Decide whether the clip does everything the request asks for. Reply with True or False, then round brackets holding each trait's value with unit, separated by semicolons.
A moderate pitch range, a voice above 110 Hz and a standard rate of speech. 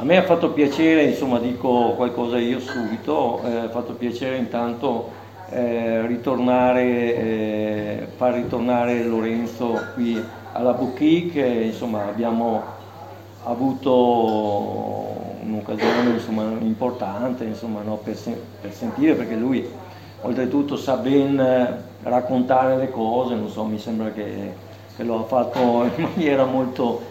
False (2.1 semitones; 120 Hz; 125 wpm)